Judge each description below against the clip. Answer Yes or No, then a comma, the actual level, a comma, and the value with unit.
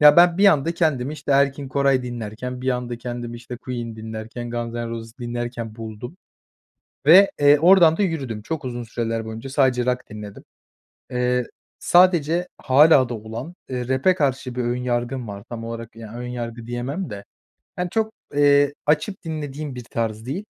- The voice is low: Yes, low, 125 Hz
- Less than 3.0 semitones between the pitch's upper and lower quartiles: No, average, 3.8 semitones